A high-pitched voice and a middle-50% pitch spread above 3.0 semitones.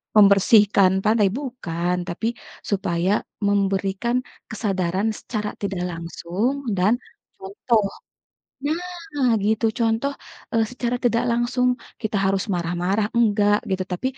Yes: high, 205 Hz; average, 3.7 semitones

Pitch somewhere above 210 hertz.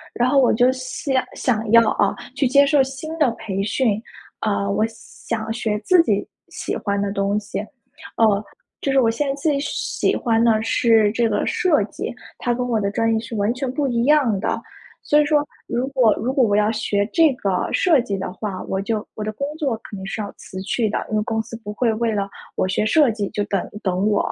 Yes: high, 225 Hz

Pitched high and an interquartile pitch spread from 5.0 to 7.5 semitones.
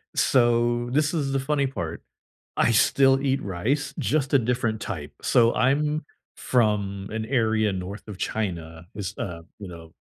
No: low, 115 Hz; wide, 5.5 semitones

